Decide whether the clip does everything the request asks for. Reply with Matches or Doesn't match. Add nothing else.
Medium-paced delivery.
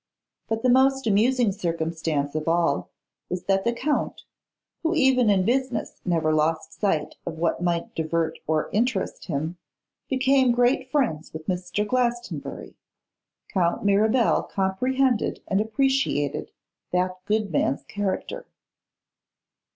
Doesn't match